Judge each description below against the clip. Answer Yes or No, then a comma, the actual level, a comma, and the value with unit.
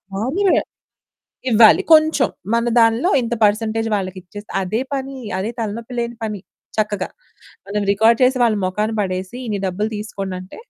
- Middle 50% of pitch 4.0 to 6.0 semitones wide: No, average, 2.8 semitones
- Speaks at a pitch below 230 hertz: Yes, high, 220 Hz